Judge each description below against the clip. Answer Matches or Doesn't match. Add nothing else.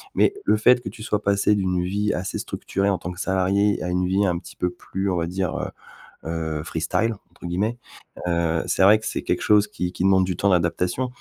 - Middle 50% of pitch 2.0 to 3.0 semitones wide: Matches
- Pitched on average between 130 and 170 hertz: Doesn't match